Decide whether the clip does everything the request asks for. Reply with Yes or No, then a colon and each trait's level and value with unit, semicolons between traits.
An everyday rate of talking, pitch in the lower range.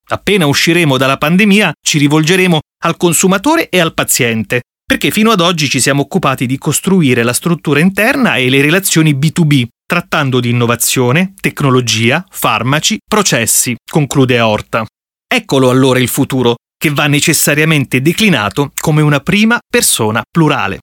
No: average, 140 wpm; medium, 150 Hz